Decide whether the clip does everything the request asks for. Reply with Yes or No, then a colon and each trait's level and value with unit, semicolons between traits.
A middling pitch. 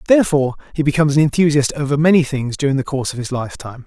Yes: medium, 145 Hz